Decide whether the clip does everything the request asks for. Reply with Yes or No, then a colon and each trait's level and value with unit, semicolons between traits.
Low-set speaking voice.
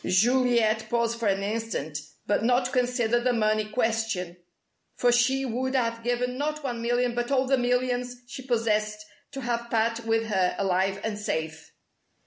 No: high, 235 Hz